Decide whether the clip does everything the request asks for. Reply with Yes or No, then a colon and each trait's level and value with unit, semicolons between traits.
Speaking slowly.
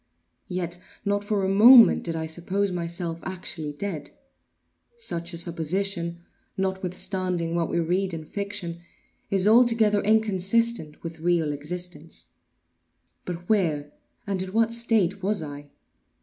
Yes: slow, 120 wpm